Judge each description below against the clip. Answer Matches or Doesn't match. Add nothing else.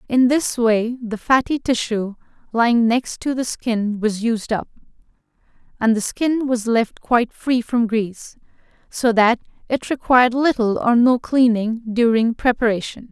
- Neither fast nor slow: Matches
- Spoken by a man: Doesn't match